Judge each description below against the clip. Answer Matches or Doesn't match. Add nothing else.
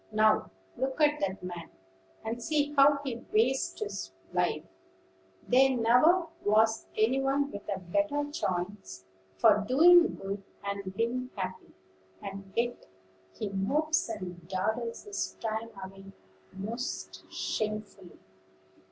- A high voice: Matches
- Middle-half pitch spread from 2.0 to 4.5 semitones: Doesn't match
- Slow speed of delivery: Matches